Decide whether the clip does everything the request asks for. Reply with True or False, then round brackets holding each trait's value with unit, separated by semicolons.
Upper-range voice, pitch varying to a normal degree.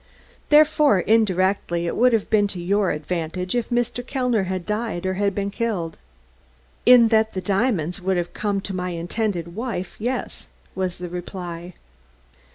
True (195 Hz; 4.1 semitones)